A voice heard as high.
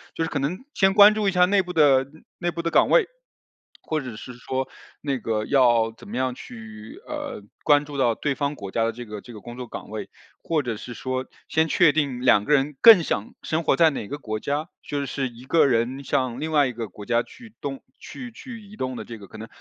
No: low, 135 Hz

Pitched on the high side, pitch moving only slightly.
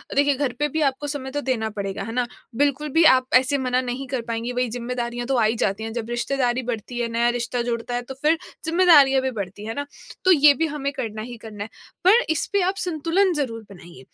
No: very high, 255 Hz; average, 3.7 semitones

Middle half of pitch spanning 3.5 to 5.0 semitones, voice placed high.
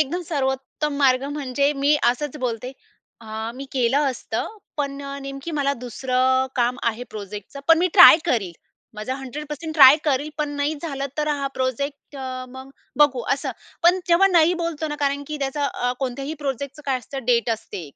No: average, 2.7 semitones; very high, 275 Hz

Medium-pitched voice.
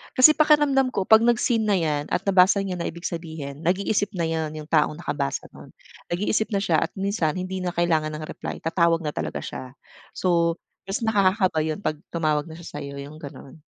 Yes: medium, 175 Hz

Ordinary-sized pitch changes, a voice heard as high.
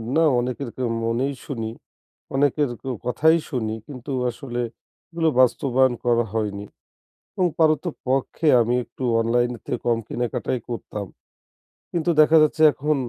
No: average, 3.9 semitones; low, 130 Hz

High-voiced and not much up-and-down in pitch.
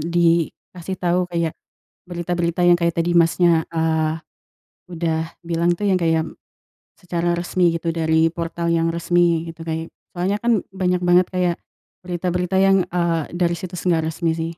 No: medium, 170 Hz; narrow, 1.3 semitones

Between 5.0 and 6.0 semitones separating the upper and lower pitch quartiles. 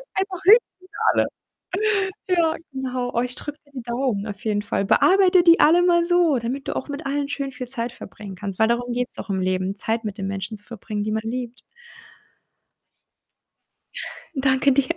Yes: average, 5.3 semitones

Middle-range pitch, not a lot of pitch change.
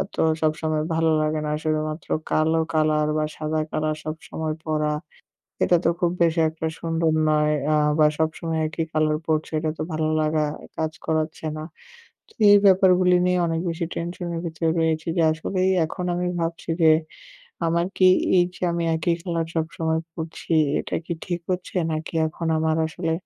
Yes: medium, 160 Hz; narrow, 1.4 semitones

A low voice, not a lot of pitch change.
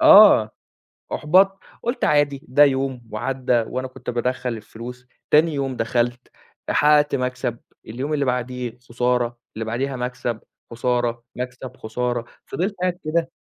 No: low, 125 Hz; average, 3.0 semitones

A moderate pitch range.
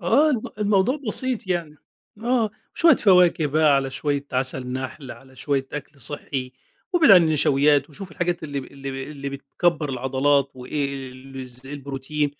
Yes: average, 4.5 semitones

